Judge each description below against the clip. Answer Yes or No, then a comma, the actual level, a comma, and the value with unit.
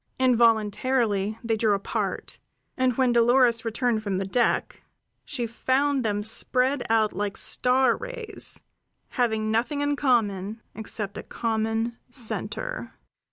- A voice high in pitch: Yes, high, 235 Hz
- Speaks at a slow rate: Yes, slow, 120 wpm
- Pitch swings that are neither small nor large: Yes, average, 3.0 semitones